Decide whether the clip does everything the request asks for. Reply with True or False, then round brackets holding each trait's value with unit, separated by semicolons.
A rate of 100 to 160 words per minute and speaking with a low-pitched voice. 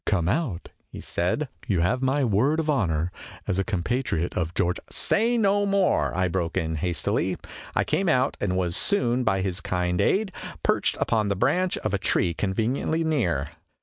False (200 wpm; 100 Hz)